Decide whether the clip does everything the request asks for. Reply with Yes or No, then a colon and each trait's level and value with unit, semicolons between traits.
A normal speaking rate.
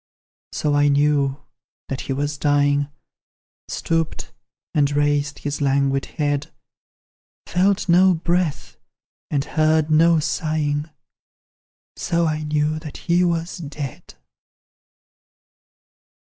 No: slow, 100 wpm